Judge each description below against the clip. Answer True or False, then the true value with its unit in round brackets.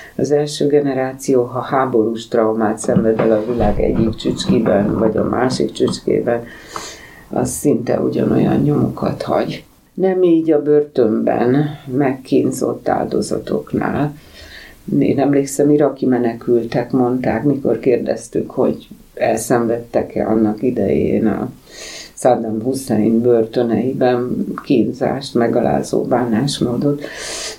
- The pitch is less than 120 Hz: False (125 Hz)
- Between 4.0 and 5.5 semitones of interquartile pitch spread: False (3.3 semitones)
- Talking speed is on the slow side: True (100 wpm)